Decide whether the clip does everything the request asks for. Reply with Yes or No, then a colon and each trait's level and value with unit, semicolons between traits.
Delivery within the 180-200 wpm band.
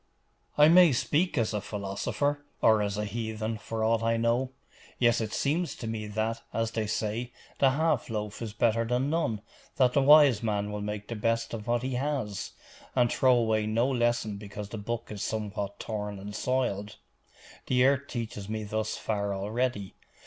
Yes: average, 185 wpm